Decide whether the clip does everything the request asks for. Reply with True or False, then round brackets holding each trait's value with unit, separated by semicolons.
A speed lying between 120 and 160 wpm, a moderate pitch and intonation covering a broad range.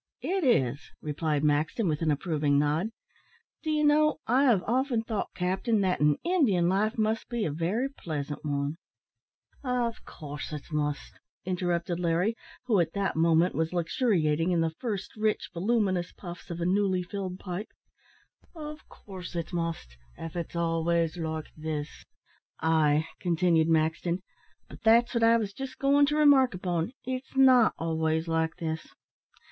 True (155 wpm; 175 Hz; 5.9 semitones)